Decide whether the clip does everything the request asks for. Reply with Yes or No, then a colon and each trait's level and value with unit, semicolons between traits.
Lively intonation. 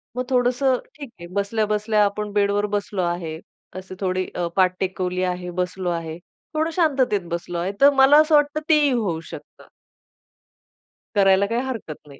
Yes: wide, 5.7 semitones